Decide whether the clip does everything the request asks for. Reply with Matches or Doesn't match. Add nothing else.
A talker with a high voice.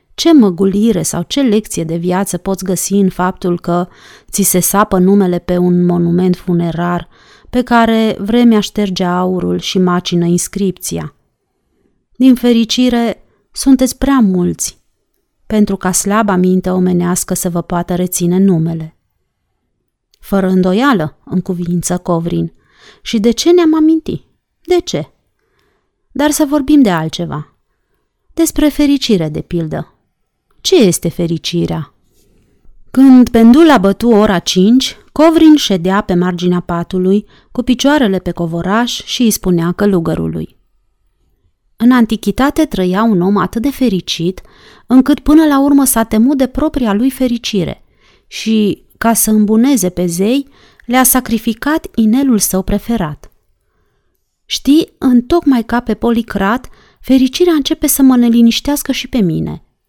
Matches